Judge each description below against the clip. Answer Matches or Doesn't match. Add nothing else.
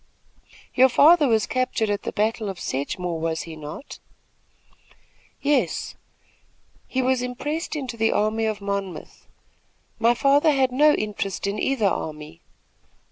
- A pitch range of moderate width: Matches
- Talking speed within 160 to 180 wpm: Doesn't match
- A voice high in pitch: Matches